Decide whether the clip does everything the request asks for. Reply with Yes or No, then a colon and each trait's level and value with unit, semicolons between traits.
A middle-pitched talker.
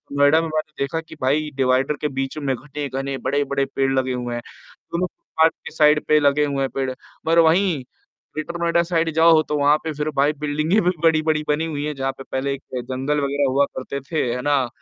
Yes: medium, 145 Hz